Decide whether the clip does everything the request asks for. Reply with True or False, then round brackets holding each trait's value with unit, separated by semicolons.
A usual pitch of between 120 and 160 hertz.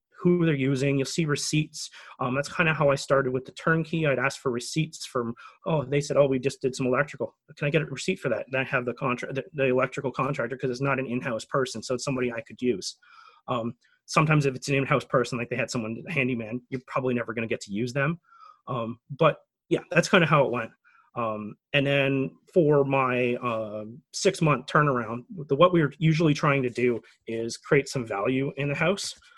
True (135 Hz)